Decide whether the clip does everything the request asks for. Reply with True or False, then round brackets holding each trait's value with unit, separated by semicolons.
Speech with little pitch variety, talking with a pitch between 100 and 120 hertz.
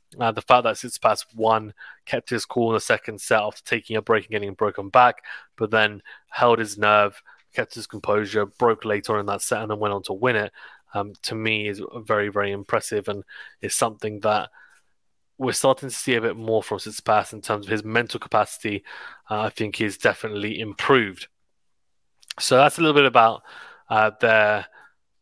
True (1.4 semitones; 110 Hz)